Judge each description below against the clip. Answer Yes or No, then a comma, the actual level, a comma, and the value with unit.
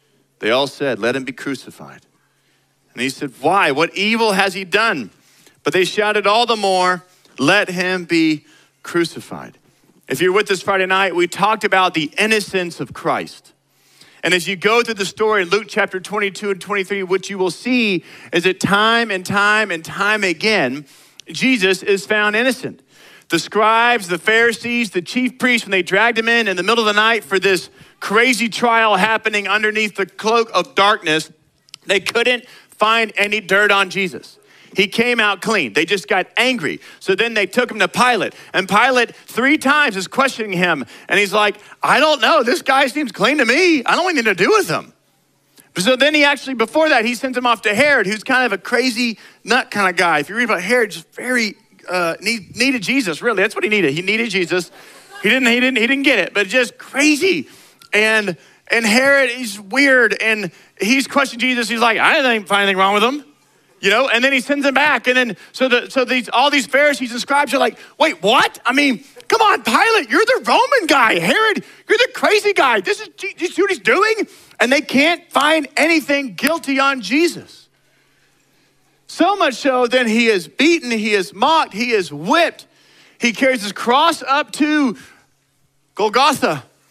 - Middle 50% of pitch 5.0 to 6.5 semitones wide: Yes, average, 5.3 semitones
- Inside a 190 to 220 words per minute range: Yes, average, 195 wpm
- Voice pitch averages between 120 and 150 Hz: No, high, 225 Hz